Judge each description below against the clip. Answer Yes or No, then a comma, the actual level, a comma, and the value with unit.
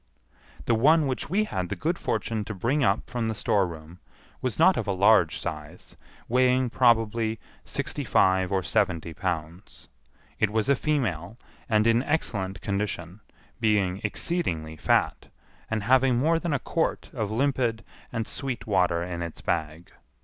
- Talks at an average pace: Yes, average, 155 wpm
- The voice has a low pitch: Yes, low, 110 Hz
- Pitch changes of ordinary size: No, wide, 5.8 semitones